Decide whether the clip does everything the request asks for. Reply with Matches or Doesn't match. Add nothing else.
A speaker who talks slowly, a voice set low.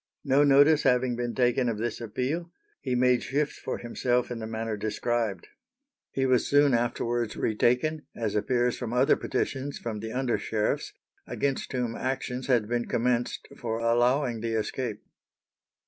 Doesn't match